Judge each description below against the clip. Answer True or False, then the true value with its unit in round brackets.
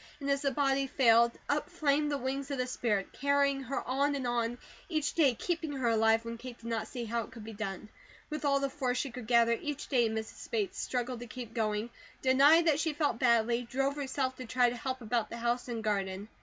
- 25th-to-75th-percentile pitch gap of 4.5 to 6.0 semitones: False (3.2 semitones)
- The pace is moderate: False (230 wpm)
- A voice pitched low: False (250 Hz)